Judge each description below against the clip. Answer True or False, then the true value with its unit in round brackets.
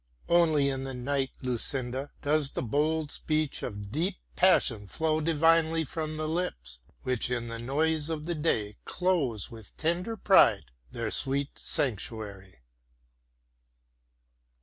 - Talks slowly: True (125 wpm)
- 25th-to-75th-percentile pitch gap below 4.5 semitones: False (5.2 semitones)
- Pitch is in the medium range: True (145 Hz)